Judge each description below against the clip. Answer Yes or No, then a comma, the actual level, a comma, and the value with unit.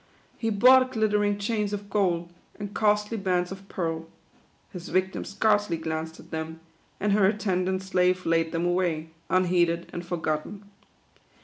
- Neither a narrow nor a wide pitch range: Yes, average, 3.4 semitones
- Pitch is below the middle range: No, medium, 185 Hz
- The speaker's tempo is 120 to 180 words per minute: Yes, average, 145 wpm